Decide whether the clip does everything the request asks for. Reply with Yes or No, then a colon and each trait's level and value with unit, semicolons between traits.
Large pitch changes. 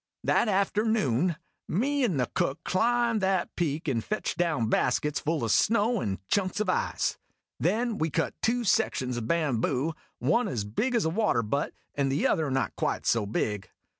Yes: wide, 8.9 semitones